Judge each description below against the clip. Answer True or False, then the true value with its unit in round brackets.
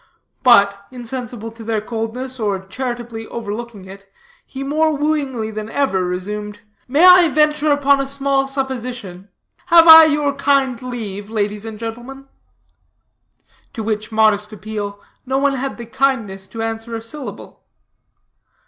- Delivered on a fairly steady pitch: False (4.4 semitones)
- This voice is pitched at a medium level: False (235 Hz)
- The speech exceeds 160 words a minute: False (140 wpm)